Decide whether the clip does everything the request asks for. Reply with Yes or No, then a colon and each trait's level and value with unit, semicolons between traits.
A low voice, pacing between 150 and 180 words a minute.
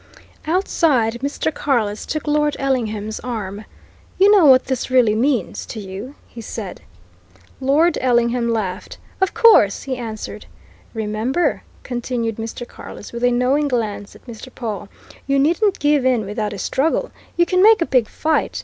No: high, 245 Hz; average, 155 wpm